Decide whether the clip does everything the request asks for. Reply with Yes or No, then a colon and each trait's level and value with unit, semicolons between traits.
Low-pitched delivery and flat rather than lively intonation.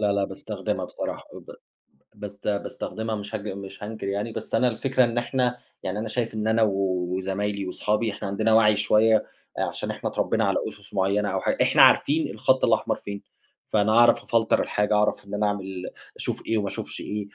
Yes: low, 105 Hz; narrow, 2.0 semitones